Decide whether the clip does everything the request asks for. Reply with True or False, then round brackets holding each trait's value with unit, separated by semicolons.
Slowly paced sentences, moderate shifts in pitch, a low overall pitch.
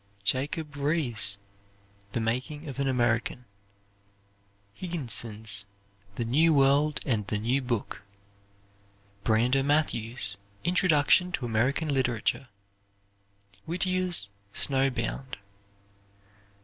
True (85 wpm; 4.6 semitones; 130 Hz)